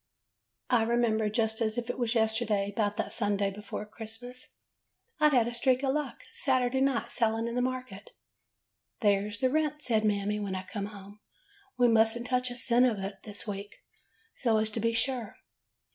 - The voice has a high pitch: Yes, high, 225 Hz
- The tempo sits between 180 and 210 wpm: Yes, average, 195 wpm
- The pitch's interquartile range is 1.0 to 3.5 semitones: Yes, average, 3.0 semitones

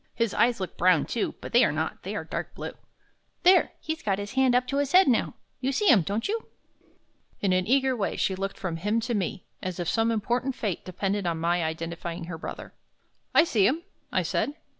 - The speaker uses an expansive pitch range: Yes, wide, 5.9 semitones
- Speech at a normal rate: No, fast, 220 wpm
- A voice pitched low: No, high, 210 Hz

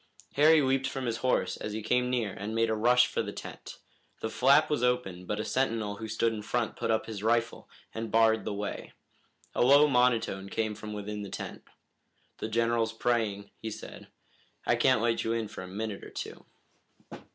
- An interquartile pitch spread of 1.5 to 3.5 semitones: Yes, narrow, 2.6 semitones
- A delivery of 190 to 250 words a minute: Yes, average, 200 wpm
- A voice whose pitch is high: No, low, 115 Hz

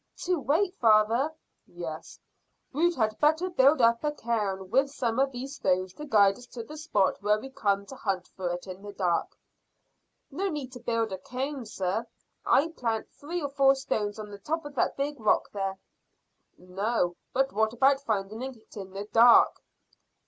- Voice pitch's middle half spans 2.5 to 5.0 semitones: No, wide, 5.5 semitones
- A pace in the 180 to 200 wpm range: Yes, average, 185 wpm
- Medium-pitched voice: No, high, 230 Hz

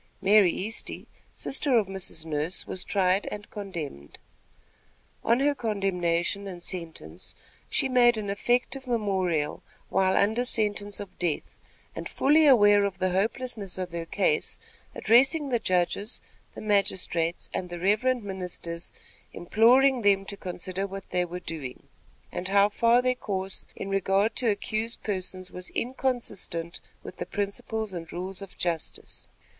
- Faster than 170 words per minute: No, average, 140 wpm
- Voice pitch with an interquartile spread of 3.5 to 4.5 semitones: Yes, average, 3.8 semitones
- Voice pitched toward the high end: Yes, high, 195 Hz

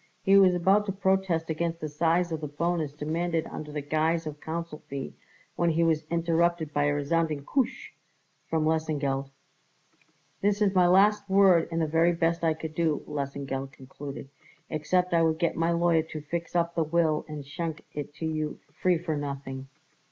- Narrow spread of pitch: Yes, narrow, 2.2 semitones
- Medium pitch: Yes, medium, 160 Hz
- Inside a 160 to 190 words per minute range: Yes, average, 180 wpm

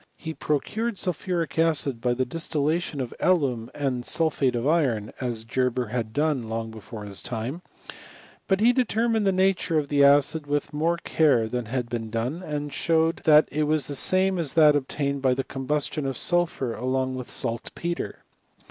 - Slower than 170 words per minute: No, average, 185 wpm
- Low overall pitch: No, medium, 145 Hz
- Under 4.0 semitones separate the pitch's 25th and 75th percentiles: No, average, 4.7 semitones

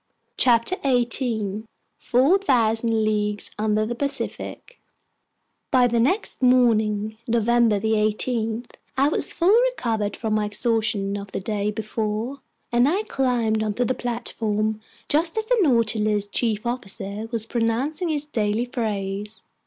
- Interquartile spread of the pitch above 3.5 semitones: No, average, 2.9 semitones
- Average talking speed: No, slow, 130 wpm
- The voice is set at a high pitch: Yes, high, 225 Hz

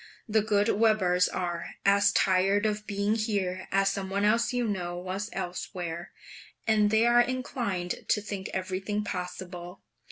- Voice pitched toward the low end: No, high, 200 Hz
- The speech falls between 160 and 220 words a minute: No, average, 150 wpm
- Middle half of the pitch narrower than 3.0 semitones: Yes, narrow, 2.6 semitones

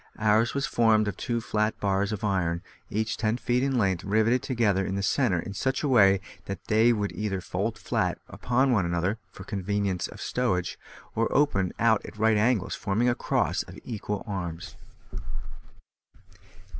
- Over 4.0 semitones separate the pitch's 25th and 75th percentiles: No, average, 3.3 semitones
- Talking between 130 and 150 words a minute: No, average, 180 wpm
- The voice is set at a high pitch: No, low, 105 Hz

